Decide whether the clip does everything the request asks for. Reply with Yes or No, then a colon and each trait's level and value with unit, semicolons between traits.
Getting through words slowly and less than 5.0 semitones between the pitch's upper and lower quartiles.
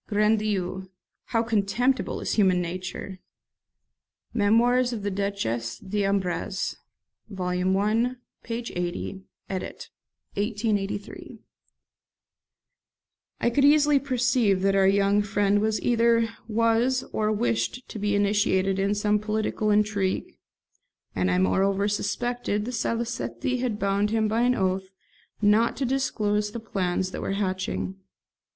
Yes: slow, 120 wpm; average, 3.0 semitones